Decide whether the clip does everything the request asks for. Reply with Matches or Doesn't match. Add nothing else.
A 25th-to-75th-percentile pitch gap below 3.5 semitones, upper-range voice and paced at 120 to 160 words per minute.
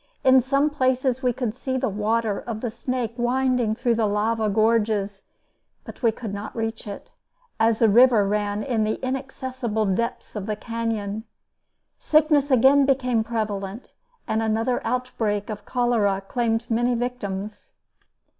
Matches